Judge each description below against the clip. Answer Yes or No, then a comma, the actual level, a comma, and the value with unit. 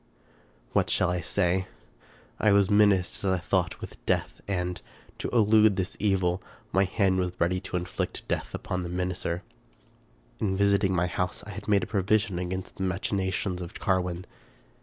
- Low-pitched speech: Yes, very low, 95 Hz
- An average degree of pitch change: No, narrow, 1.9 semitones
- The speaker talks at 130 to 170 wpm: Yes, average, 160 wpm